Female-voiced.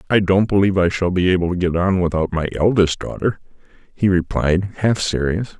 No: male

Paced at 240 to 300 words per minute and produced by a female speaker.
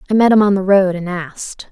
Yes: fast, 280 wpm; female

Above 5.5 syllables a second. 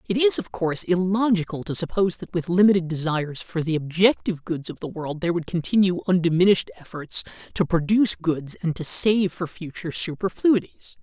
Yes: 5.8 syllables/s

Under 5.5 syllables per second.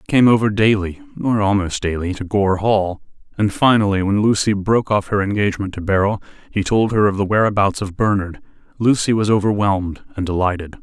No: 5.8 syllables/s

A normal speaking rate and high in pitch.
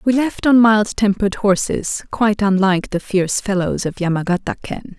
Yes: average, 170 wpm; high, 200 Hz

